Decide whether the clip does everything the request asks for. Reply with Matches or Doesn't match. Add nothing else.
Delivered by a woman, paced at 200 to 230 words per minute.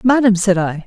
Matches